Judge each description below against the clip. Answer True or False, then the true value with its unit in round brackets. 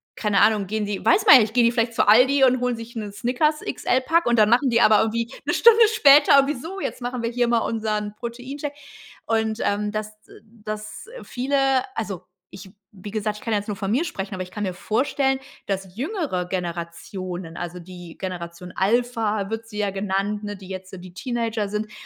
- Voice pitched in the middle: False (215 Hz)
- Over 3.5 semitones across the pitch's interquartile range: True (3.9 semitones)